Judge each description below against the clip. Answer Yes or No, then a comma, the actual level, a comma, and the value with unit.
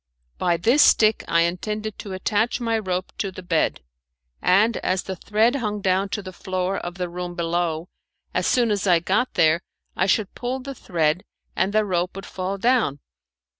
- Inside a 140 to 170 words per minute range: No, average, 185 wpm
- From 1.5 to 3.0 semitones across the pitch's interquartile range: No, average, 3.4 semitones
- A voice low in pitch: No, high, 190 Hz